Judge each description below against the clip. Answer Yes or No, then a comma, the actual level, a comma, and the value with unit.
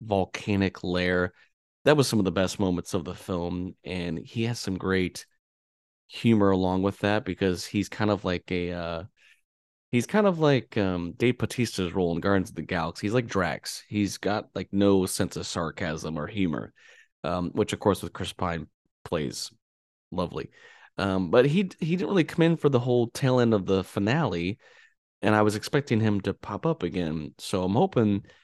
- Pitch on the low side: Yes, very low, 95 Hz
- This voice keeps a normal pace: Yes, average, 190 wpm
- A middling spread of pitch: Yes, average, 4.1 semitones